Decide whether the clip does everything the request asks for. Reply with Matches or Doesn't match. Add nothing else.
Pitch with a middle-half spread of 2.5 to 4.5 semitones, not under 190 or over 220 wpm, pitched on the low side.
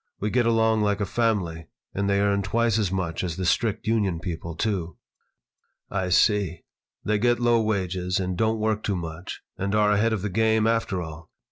Matches